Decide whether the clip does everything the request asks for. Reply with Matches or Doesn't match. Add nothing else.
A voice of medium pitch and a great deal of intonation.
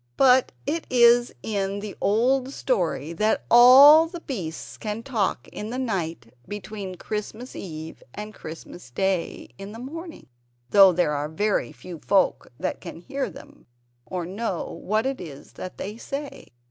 Doesn't match